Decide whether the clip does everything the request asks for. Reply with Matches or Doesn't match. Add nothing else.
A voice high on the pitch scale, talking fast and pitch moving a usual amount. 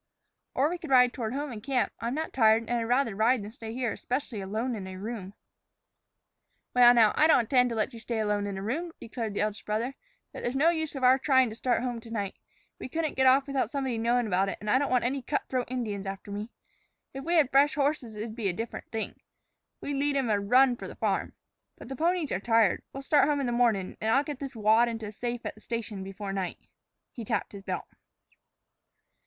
Matches